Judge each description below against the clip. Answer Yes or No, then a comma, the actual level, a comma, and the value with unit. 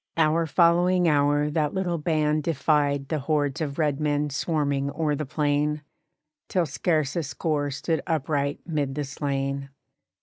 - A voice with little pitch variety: Yes, narrow, 2.1 semitones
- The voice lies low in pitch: No, medium, 150 Hz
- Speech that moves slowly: No, average, 145 wpm